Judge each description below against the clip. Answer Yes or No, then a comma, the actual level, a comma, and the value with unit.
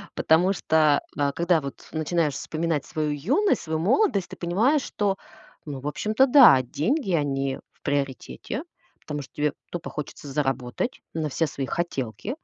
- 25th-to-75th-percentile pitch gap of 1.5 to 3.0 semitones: No, average, 5.1 semitones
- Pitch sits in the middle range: Yes, medium, 155 Hz